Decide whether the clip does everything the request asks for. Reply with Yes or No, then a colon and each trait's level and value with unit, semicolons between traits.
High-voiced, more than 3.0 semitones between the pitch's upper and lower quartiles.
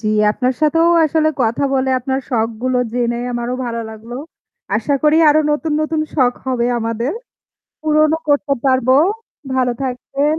Yes: very high, 260 Hz; average, 4.1 semitones